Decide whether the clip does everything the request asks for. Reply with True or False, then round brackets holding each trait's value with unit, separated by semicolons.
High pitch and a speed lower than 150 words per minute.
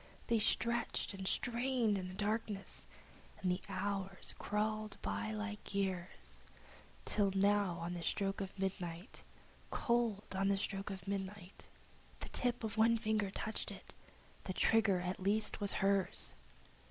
True (200 Hz; 140 wpm)